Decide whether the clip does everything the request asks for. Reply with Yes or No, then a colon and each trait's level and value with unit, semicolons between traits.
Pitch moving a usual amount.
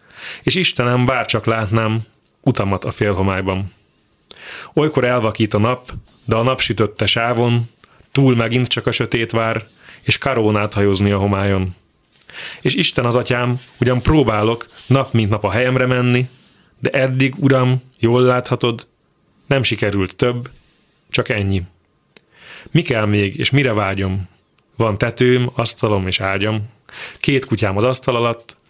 Yes: average, 3.1 semitones